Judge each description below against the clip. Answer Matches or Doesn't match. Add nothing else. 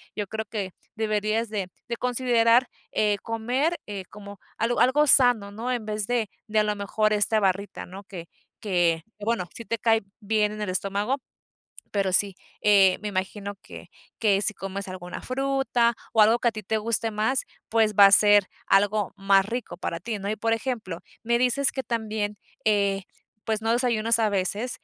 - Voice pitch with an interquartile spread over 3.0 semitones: Doesn't match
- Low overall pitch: Doesn't match